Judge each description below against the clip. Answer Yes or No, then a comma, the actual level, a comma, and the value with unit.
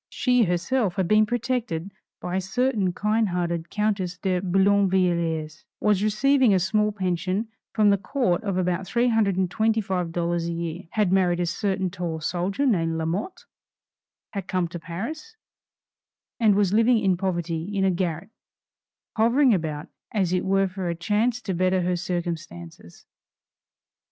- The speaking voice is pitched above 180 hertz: Yes, high, 190 Hz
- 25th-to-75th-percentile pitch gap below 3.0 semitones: No, average, 3.5 semitones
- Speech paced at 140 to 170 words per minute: Yes, average, 145 wpm